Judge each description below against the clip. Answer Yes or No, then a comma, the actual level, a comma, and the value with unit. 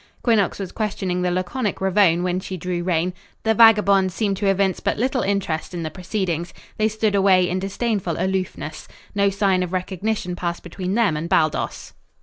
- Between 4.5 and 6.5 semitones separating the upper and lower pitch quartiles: No, narrow, 2.4 semitones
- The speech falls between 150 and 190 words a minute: Yes, average, 175 wpm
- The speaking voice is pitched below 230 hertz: Yes, high, 190 Hz